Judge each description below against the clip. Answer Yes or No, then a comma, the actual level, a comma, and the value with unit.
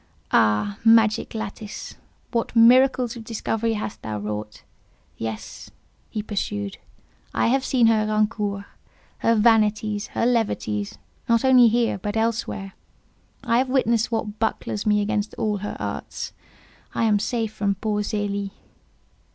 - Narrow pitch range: Yes, narrow, 2.2 semitones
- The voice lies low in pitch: No, high, 215 Hz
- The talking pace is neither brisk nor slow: No, slow, 130 wpm